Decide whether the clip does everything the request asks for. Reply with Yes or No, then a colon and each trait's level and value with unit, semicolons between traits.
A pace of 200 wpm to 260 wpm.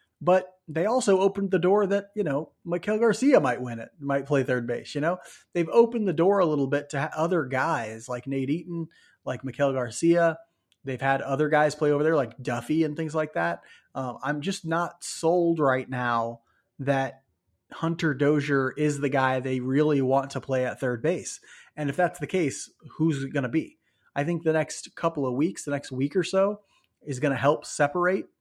Yes: fast, 205 wpm